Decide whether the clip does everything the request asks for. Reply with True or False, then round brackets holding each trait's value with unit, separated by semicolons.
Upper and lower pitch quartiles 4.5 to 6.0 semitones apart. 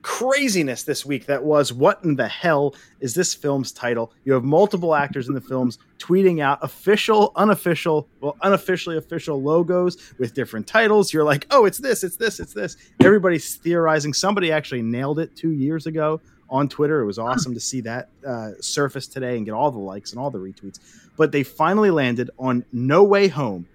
True (5.0 semitones)